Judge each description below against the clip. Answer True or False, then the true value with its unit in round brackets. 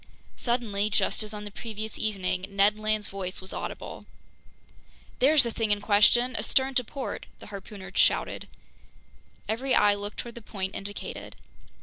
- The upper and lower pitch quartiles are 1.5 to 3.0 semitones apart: True (2.7 semitones)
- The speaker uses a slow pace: False (150 wpm)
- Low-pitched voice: False (210 Hz)